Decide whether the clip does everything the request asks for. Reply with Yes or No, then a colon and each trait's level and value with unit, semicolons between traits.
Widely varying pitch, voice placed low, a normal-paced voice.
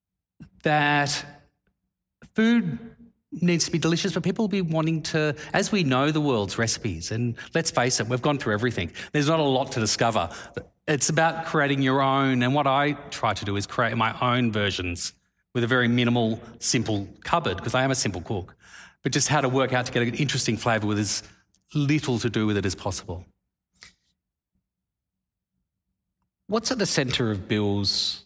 Yes: wide, 6.1 semitones; low, 125 Hz; average, 185 wpm